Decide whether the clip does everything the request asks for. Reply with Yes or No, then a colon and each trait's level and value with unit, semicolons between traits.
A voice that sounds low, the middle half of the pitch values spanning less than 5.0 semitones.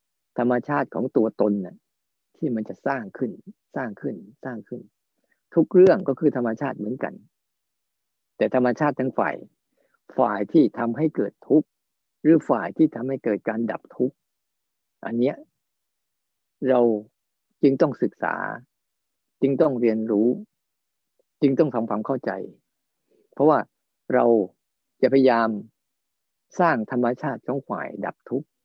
Yes: low, 125 Hz; average, 4.3 semitones